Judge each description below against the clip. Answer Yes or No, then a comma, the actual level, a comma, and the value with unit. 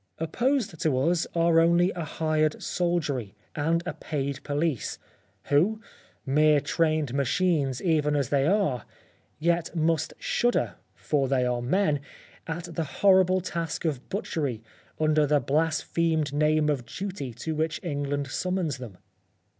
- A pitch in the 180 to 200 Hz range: No, medium, 155 Hz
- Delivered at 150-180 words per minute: No, slow, 135 wpm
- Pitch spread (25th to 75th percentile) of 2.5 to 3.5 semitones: Yes, average, 3.1 semitones